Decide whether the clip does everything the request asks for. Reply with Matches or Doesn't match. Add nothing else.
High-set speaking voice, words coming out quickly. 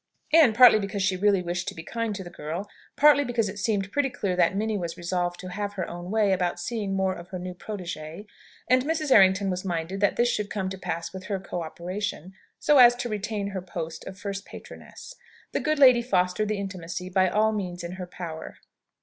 Matches